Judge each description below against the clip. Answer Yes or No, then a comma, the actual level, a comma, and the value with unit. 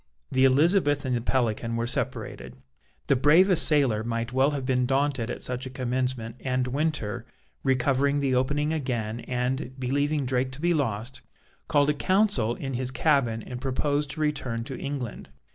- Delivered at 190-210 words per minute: No, average, 165 wpm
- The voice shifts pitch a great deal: No, average, 2.8 semitones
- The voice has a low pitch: Yes, low, 130 Hz